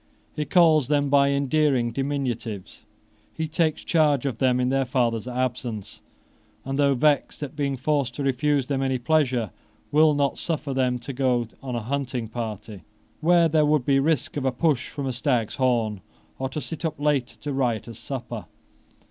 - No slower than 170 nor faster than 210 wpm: Yes, average, 180 wpm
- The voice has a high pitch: No, low, 135 Hz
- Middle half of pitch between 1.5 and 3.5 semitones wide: Yes, average, 3.1 semitones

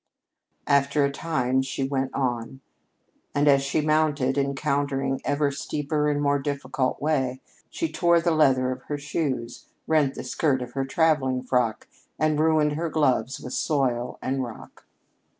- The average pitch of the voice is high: No, medium, 140 Hz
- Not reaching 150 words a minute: No, average, 155 wpm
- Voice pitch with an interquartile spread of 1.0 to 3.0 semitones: Yes, narrow, 2.4 semitones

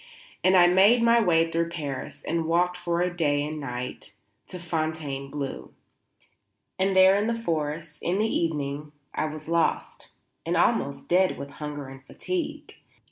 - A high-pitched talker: No, medium, 165 Hz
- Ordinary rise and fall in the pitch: Yes, average, 3.7 semitones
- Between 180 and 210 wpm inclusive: No, average, 155 wpm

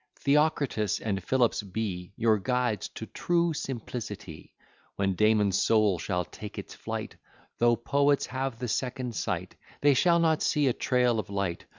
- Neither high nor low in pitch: No, low, 115 Hz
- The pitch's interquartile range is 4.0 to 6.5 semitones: Yes, average, 4.8 semitones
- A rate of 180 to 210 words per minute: No, average, 155 wpm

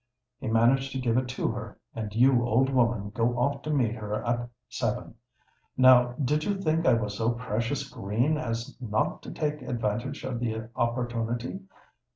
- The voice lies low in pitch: Yes, low, 120 Hz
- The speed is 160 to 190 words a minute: Yes, average, 175 wpm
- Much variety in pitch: No, average, 2.7 semitones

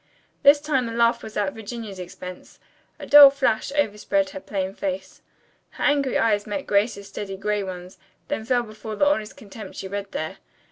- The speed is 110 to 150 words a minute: No, average, 180 wpm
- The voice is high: Yes, high, 215 Hz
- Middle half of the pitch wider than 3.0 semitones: Yes, average, 4.4 semitones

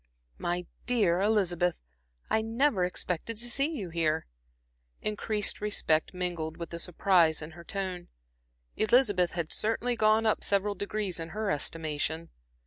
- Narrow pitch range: No, average, 4.2 semitones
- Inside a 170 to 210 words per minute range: No, slow, 135 wpm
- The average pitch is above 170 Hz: Yes, medium, 185 Hz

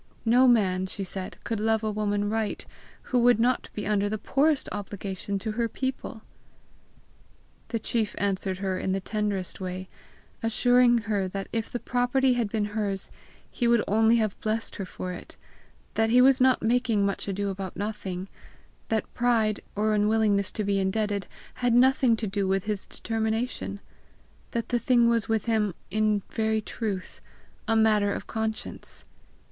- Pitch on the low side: No, high, 215 Hz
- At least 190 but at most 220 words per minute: No, average, 165 wpm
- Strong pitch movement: No, narrow, 2.6 semitones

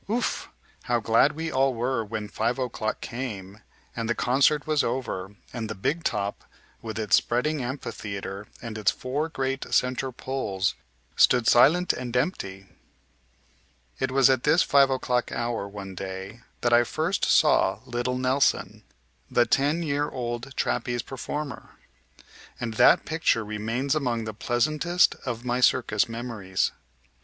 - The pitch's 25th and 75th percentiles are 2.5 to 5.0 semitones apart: Yes, average, 3.6 semitones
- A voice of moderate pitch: No, low, 120 Hz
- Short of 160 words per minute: Yes, average, 145 wpm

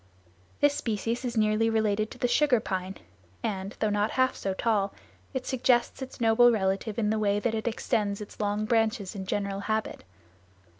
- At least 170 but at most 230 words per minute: Yes, average, 180 wpm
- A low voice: No, high, 215 Hz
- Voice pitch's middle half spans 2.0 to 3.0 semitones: Yes, narrow, 2.6 semitones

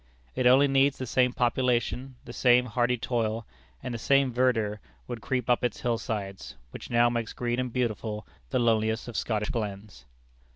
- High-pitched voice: No, low, 120 Hz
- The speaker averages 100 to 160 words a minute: No, average, 175 wpm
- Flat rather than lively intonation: Yes, narrow, 2.3 semitones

